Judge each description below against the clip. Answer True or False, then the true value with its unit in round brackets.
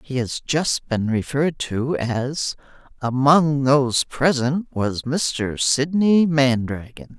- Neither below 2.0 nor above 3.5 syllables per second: True (3.3 syllables/s)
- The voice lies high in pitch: False (140 Hz)